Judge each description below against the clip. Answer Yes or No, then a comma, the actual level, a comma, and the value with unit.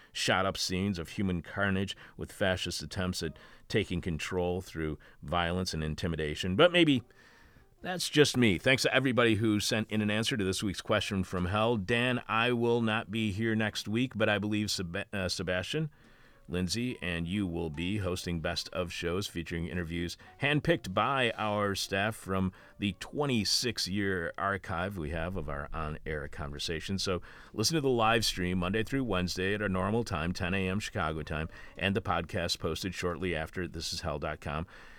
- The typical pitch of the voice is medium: No, very low, 95 Hz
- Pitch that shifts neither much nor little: Yes, average, 4.0 semitones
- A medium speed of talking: Yes, average, 175 wpm